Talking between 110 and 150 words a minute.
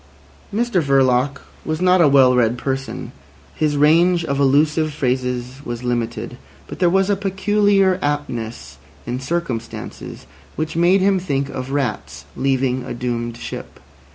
Yes: average, 140 wpm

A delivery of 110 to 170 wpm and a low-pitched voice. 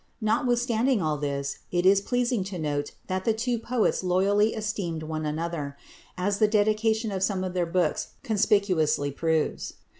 No: average, 155 wpm; high, 190 Hz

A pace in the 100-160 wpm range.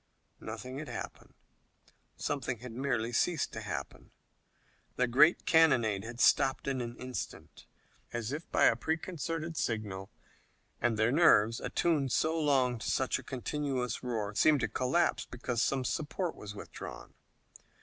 Yes: average, 140 wpm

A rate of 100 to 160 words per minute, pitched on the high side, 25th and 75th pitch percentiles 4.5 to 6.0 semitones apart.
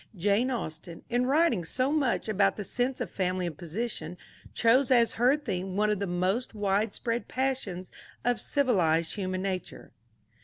Yes: average, 155 wpm; high, 210 Hz; average, 5.2 semitones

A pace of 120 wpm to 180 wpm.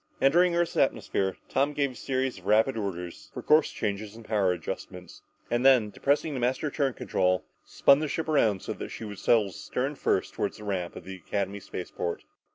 No: average, 195 wpm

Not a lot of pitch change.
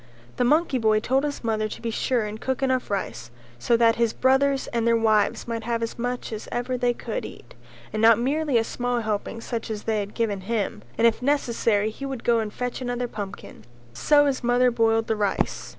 Yes: narrow, 2.3 semitones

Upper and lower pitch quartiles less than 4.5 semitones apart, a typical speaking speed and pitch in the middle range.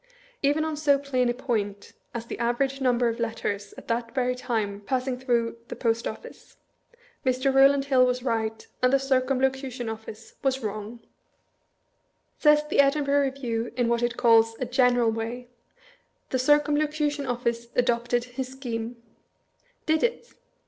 No: average, 2.8 semitones; average, 155 wpm; very high, 250 Hz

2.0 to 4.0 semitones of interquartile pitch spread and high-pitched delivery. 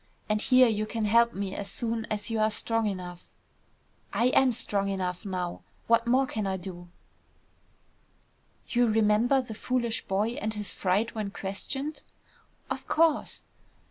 Yes: average, 3.2 semitones; high, 215 Hz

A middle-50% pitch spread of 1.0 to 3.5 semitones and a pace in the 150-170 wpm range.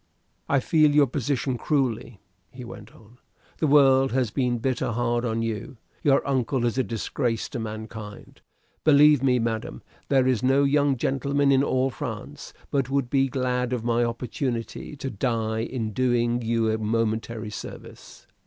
Yes: average, 3.0 semitones; average, 160 wpm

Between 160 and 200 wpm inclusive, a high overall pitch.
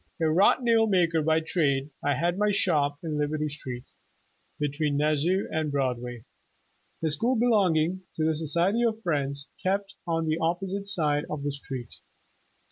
No: average, 165 wpm; medium, 160 Hz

